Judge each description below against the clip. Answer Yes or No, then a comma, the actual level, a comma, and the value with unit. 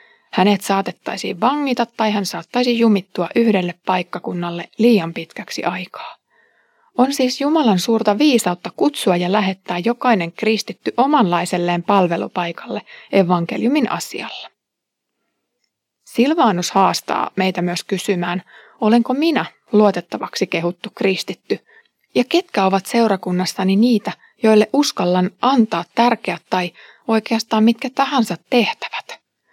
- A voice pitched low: No, high, 210 Hz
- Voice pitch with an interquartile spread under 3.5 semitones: No, average, 4.9 semitones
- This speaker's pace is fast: No, average, 100 wpm